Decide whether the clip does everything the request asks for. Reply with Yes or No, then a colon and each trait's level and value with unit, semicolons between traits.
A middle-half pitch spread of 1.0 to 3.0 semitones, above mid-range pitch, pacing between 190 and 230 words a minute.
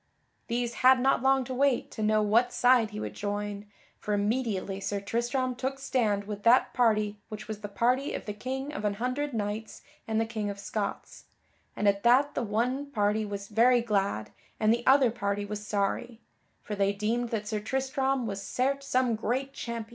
No: average, 3.5 semitones; high, 225 Hz; average, 195 wpm